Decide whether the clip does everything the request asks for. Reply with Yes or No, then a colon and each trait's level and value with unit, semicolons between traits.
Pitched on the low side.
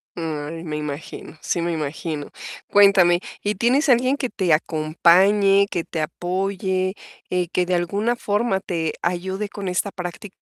No: medium, 180 Hz